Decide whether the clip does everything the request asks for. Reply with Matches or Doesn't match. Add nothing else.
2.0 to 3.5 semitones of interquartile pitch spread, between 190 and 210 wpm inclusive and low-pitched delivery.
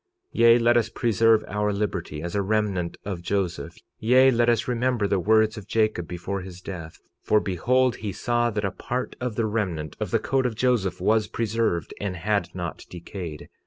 Doesn't match